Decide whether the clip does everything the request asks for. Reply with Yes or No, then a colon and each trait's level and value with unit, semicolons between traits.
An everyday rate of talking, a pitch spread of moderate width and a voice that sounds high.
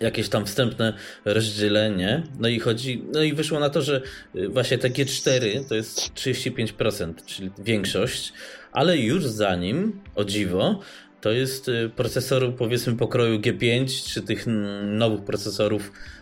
No: average, 135 wpm; average, 3.5 semitones; low, 115 Hz